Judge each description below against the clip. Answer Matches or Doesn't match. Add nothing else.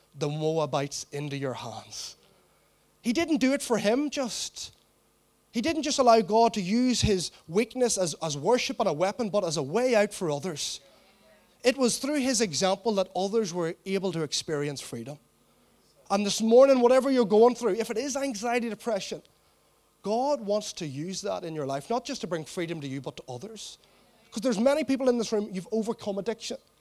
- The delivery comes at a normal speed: Matches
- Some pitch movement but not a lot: Doesn't match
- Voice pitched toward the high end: Matches